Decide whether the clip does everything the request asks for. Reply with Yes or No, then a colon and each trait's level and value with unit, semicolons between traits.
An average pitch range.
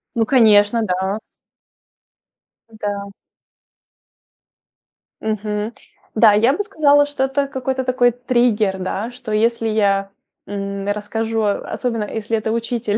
Yes: average, 3.0 semitones